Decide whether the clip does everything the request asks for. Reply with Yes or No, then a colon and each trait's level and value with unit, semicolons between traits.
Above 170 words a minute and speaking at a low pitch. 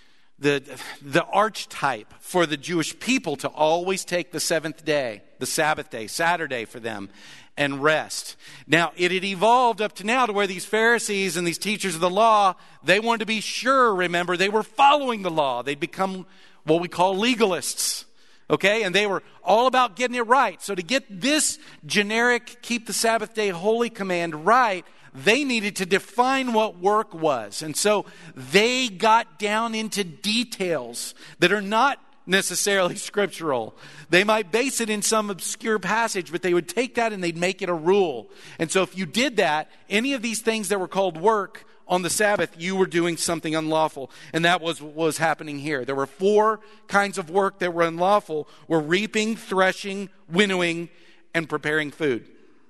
No: average, 180 wpm; high, 190 Hz